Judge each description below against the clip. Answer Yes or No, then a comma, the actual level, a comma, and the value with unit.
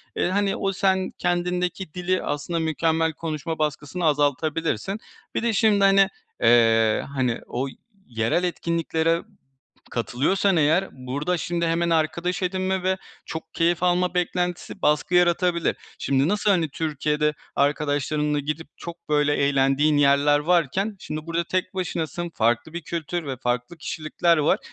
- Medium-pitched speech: Yes, medium, 165 Hz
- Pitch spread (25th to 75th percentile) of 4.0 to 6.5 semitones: No, average, 3.5 semitones